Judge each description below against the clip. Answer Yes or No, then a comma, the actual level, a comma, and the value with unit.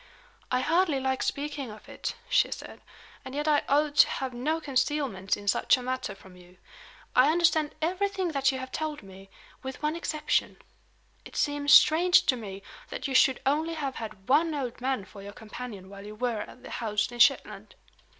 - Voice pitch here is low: No, very high, 265 Hz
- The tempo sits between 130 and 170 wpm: No, average, 190 wpm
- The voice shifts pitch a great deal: Yes, wide, 5.7 semitones